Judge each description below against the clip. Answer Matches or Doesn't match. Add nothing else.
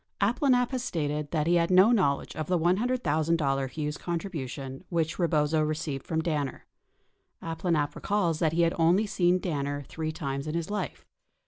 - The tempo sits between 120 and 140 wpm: Doesn't match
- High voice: Doesn't match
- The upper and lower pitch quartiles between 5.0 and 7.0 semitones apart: Doesn't match